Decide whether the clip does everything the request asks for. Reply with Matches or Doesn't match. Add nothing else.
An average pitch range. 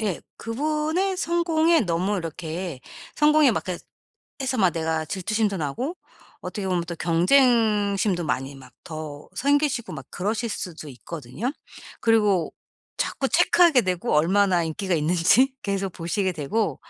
Doesn't match